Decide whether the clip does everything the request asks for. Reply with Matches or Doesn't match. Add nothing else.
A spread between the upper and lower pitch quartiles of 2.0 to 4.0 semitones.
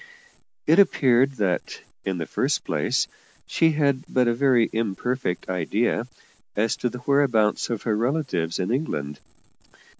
Doesn't match